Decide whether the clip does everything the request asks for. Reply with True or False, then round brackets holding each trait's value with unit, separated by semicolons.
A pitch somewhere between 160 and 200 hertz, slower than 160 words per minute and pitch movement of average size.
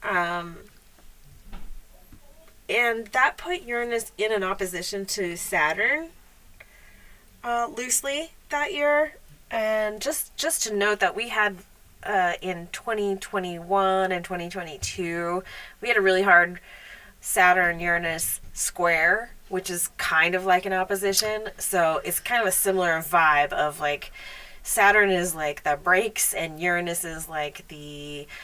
True (185 Hz; 135 wpm; 3.8 semitones)